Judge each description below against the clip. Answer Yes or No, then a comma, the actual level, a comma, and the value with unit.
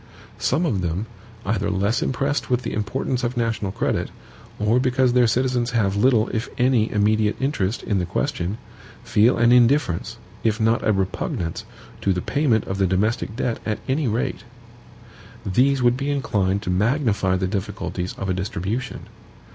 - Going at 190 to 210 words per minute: No, average, 165 wpm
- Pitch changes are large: No, average, 4.3 semitones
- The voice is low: Yes, low, 110 Hz